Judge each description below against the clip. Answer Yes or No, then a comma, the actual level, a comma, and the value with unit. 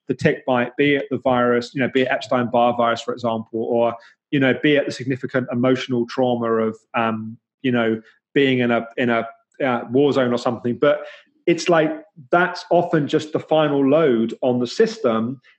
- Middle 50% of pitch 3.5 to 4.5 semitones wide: Yes, average, 3.8 semitones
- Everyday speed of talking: Yes, average, 190 wpm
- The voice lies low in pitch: Yes, low, 130 Hz